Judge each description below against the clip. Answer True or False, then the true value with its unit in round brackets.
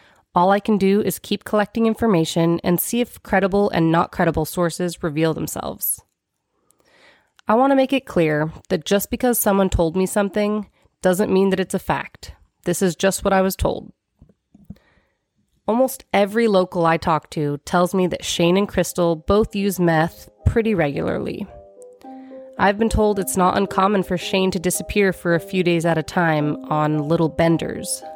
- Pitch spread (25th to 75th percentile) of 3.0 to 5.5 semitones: True (3.6 semitones)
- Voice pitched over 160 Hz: True (185 Hz)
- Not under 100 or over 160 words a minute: False (175 wpm)